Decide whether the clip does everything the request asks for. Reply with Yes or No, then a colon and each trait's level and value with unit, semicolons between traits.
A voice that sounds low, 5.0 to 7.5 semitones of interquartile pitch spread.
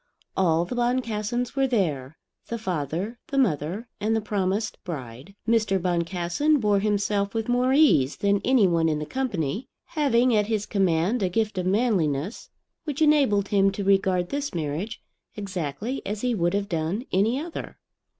No: high, 200 Hz; average, 5.3 semitones